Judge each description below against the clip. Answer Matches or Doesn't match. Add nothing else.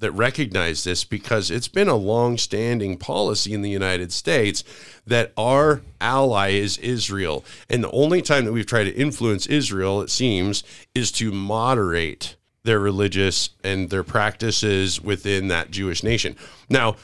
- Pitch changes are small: Doesn't match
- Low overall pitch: Matches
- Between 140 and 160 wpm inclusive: Matches